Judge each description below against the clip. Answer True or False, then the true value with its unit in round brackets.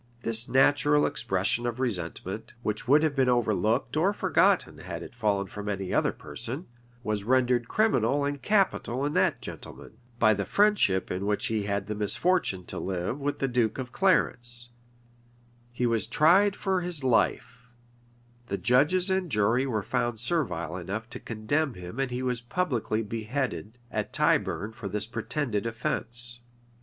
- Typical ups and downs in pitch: True (4.9 semitones)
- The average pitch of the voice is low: True (120 Hz)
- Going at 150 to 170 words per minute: True (160 wpm)